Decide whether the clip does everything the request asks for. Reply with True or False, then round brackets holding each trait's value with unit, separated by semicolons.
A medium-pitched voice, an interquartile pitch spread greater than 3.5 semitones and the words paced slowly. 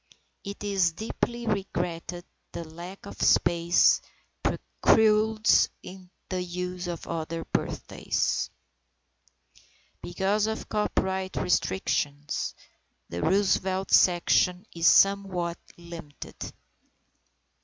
False (180 Hz; 2.7 semitones; 80 wpm)